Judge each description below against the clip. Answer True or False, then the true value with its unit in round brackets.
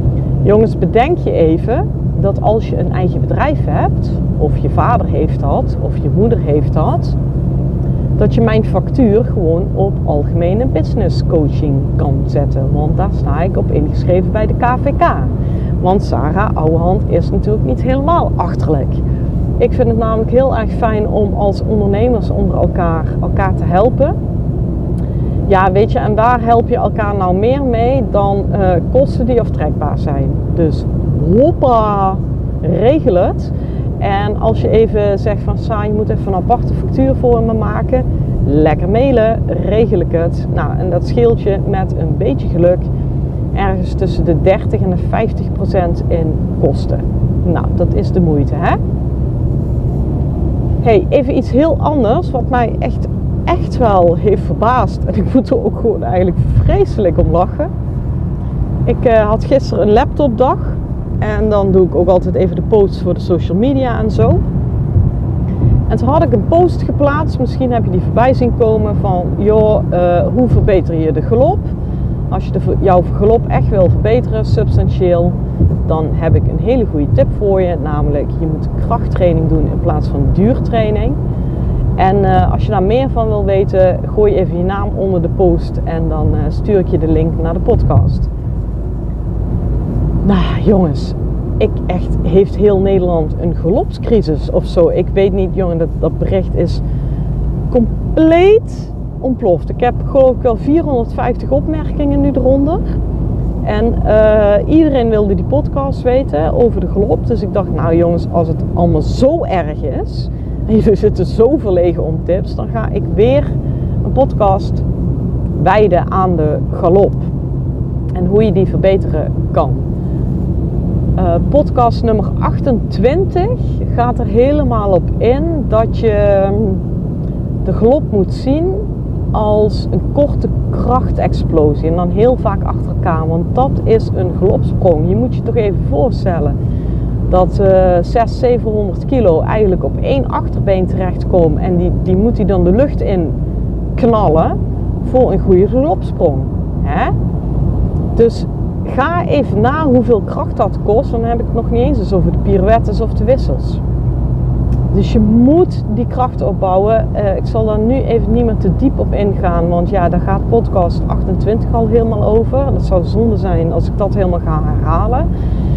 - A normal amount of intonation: False (7.9 semitones)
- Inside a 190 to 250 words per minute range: False (160 wpm)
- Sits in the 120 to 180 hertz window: True (135 Hz)